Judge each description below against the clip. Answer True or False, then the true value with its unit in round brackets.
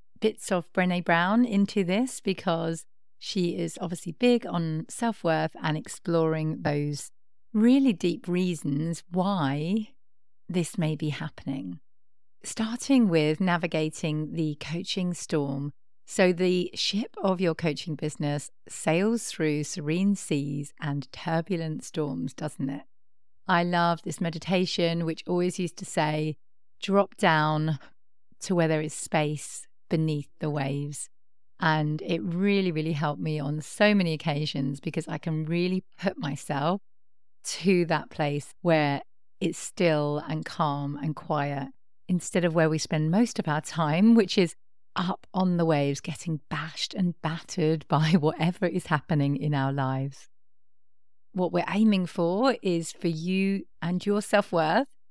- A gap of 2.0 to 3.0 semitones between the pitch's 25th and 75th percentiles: False (3.8 semitones)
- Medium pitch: True (160 Hz)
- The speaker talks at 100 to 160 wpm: True (140 wpm)